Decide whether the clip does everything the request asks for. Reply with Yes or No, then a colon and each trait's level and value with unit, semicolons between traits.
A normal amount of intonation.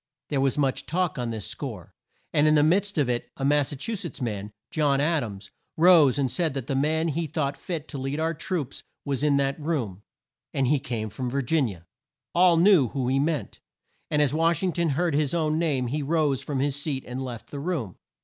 Yes: average, 3.3 semitones